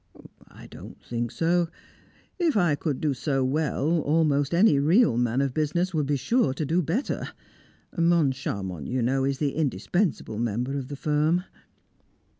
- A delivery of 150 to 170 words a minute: Yes, average, 155 wpm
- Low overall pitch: No, medium, 145 Hz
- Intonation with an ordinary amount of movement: Yes, average, 4.2 semitones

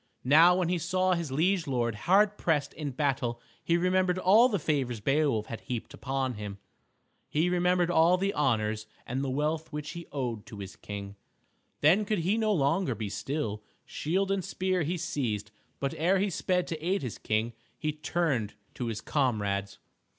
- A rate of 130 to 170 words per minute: No, average, 180 wpm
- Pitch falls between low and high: Yes, medium, 150 Hz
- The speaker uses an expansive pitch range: Yes, wide, 7.1 semitones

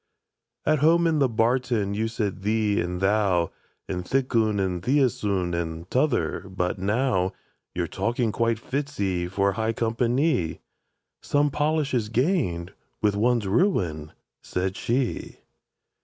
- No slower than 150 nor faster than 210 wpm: No, average, 140 wpm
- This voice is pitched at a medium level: No, low, 110 Hz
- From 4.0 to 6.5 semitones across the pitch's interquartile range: Yes, average, 5.3 semitones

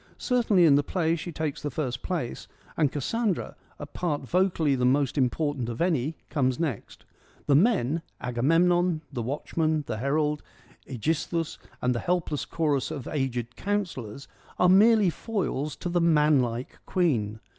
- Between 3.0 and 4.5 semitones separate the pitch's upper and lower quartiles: No, average, 5.0 semitones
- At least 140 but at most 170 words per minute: Yes, average, 155 wpm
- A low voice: No, medium, 150 Hz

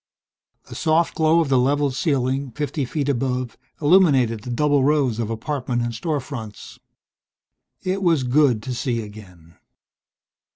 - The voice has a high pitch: No, low, 135 Hz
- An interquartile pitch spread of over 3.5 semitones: Yes, average, 4.0 semitones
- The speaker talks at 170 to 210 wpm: No, average, 140 wpm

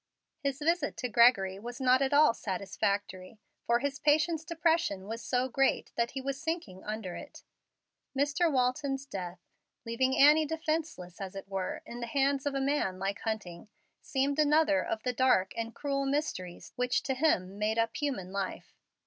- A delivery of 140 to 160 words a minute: No, average, 170 wpm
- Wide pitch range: Yes, wide, 6.2 semitones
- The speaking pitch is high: Yes, very high, 255 Hz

